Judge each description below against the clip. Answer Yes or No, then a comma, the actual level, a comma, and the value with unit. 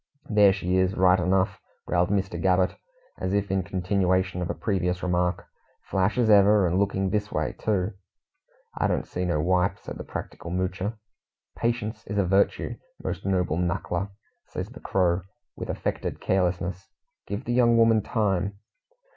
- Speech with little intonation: Yes, narrow, 2.1 semitones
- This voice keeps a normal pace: Yes, average, 160 wpm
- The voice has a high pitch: No, very low, 95 Hz